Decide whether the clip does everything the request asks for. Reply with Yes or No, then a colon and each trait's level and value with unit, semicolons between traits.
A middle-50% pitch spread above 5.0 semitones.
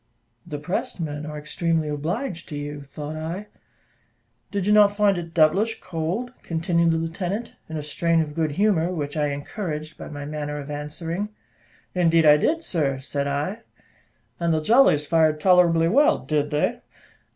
No: average, 3.6 semitones